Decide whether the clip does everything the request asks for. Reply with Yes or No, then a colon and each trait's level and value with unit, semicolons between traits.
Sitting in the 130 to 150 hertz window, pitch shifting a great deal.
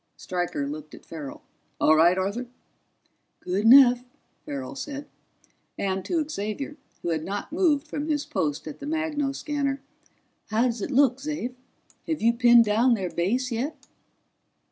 No: high, 240 Hz; wide, 7.4 semitones